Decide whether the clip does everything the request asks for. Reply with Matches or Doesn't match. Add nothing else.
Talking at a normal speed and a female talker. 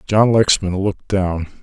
Doesn't match